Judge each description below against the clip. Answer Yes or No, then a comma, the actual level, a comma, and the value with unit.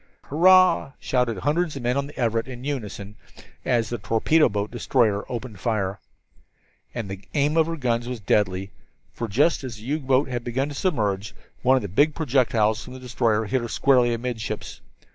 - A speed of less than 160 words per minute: No, average, 180 wpm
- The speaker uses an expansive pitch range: No, average, 4.3 semitones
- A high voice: No, low, 120 Hz